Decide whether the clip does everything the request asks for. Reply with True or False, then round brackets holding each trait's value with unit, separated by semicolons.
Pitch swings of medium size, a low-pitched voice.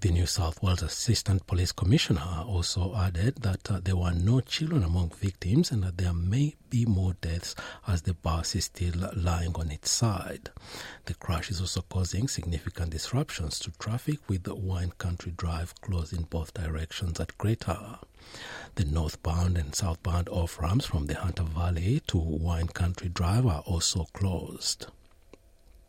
True (3.0 semitones; 90 Hz)